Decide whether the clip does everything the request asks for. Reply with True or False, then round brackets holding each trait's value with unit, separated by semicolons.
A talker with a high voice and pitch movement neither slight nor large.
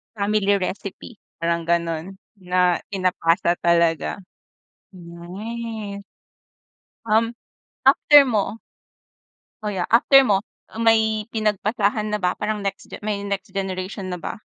True (200 Hz; 3.2 semitones)